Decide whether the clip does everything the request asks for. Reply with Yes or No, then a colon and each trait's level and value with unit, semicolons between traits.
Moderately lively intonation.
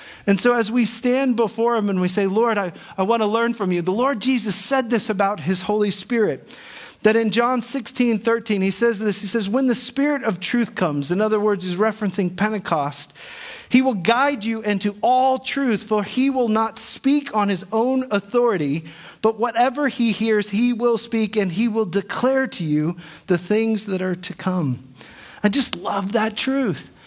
Yes: average, 3.4 semitones